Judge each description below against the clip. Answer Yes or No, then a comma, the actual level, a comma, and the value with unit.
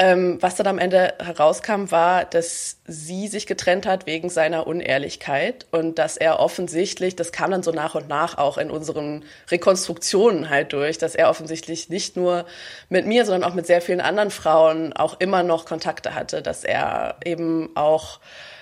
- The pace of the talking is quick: No, average, 175 wpm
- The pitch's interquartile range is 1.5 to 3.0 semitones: Yes, narrow, 2.4 semitones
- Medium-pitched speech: Yes, medium, 170 Hz